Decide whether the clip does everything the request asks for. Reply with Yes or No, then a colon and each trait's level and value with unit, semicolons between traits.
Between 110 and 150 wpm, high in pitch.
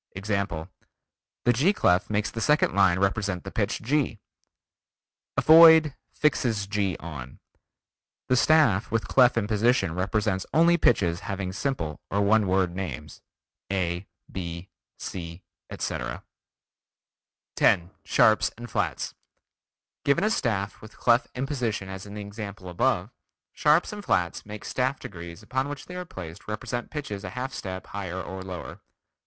No: average, 140 wpm; low, 105 Hz